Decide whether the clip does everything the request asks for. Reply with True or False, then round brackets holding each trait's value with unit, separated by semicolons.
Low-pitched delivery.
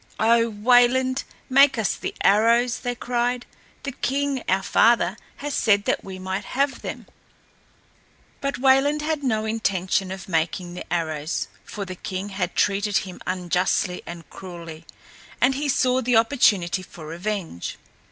False (210 Hz)